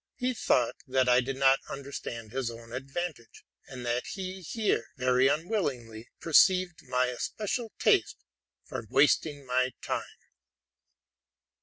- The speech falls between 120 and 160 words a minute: Yes, slow, 135 wpm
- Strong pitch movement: Yes, wide, 5.8 semitones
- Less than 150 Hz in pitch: Yes, low, 135 Hz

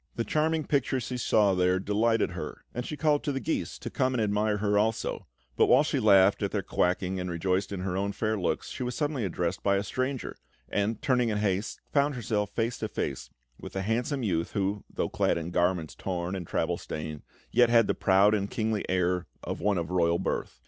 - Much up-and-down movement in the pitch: No, average, 4.6 semitones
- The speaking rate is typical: No, fast, 220 wpm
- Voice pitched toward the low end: Yes, low, 105 Hz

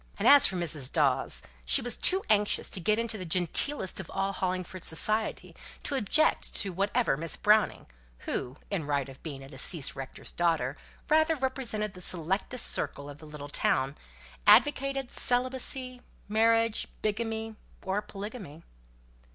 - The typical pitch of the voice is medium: No, high, 200 Hz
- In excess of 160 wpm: No, average, 150 wpm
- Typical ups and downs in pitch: No, wide, 6.5 semitones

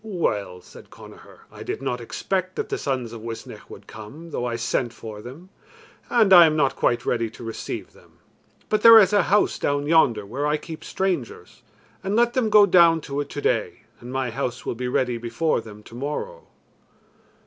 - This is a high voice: No, medium, 140 Hz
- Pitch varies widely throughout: Yes, wide, 7.2 semitones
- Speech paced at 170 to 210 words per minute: Yes, average, 190 wpm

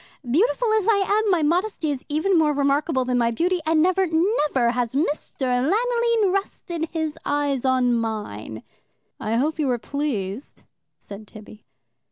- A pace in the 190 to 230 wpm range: No, average, 155 wpm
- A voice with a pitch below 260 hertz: No, very high, 295 Hz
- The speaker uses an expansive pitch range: Yes, wide, 6.6 semitones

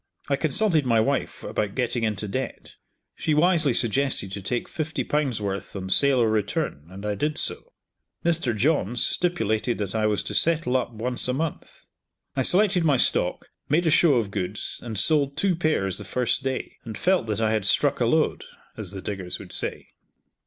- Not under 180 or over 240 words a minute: Yes, average, 190 wpm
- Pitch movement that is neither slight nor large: No, wide, 6.5 semitones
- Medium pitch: No, low, 120 Hz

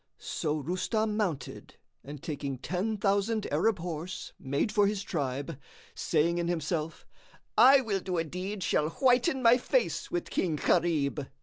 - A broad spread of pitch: Yes, wide, 5.8 semitones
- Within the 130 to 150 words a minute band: Yes, average, 145 wpm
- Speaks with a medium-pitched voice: Yes, medium, 180 Hz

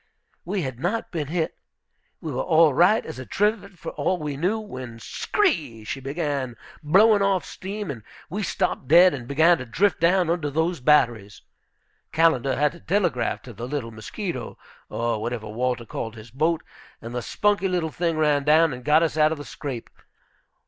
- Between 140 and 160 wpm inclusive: No, average, 185 wpm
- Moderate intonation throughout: No, wide, 5.8 semitones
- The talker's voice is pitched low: No, medium, 155 Hz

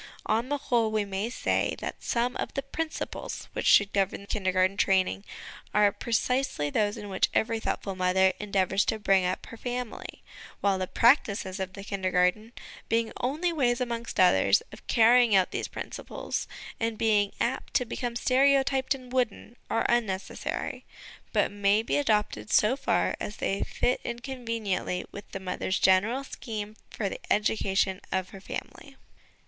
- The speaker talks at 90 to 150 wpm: No, average, 165 wpm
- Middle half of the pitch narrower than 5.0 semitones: Yes, average, 4.0 semitones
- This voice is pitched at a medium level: No, high, 215 Hz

